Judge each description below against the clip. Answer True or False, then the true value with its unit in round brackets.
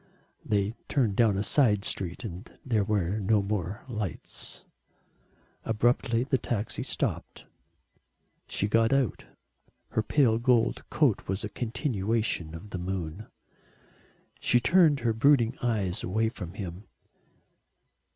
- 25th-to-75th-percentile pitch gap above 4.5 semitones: False (3.5 semitones)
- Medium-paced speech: False (120 wpm)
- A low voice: True (110 Hz)